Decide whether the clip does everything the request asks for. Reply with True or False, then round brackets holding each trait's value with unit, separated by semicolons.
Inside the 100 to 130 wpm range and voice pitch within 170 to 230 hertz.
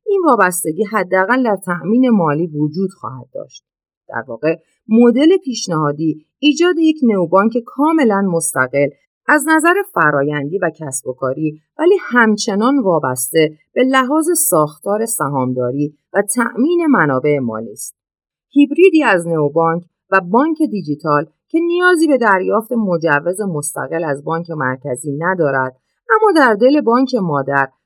True (125 wpm; 190 Hz)